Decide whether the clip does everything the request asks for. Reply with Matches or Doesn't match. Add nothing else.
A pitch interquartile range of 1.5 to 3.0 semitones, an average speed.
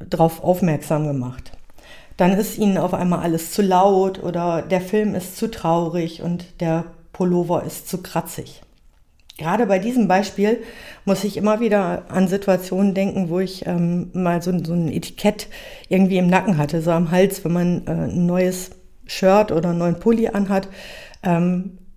Matches